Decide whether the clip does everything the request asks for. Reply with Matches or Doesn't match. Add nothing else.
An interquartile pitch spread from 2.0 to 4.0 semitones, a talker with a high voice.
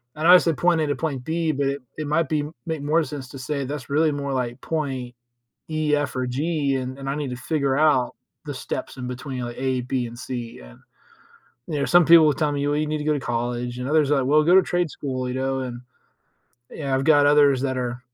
Doesn't match